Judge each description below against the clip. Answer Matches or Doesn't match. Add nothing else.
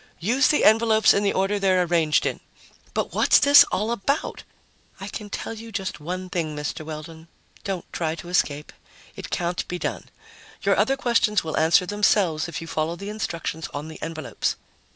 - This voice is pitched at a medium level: Matches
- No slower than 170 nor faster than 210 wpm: Matches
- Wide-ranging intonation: Doesn't match